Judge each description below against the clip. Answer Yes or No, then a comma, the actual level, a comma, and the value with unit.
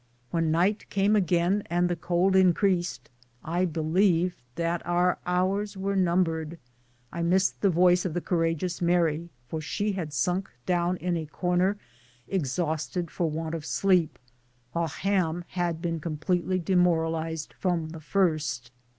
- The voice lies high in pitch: No, medium, 175 Hz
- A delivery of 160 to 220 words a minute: No, average, 145 wpm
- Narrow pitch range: Yes, narrow, 2.1 semitones